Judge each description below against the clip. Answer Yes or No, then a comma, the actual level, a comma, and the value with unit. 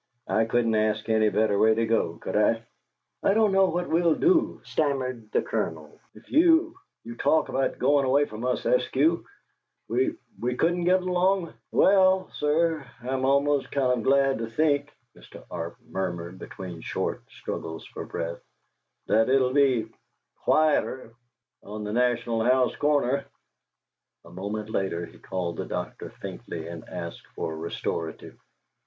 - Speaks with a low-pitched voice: Yes, low, 125 Hz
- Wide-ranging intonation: Yes, wide, 6.5 semitones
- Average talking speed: Yes, average, 155 wpm